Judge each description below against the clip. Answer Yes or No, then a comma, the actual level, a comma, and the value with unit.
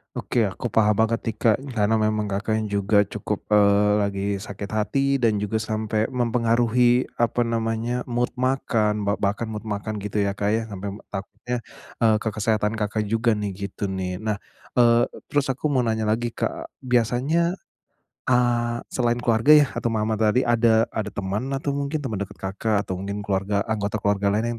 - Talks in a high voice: No, low, 110 Hz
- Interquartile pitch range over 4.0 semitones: No, narrow, 2.6 semitones